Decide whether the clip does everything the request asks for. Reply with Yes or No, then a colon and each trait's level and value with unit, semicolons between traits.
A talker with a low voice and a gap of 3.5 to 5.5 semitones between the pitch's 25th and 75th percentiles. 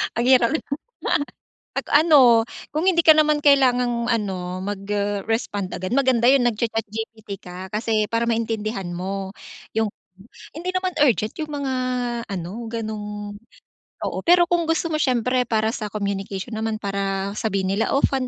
No: high, 225 Hz; average, 4.1 semitones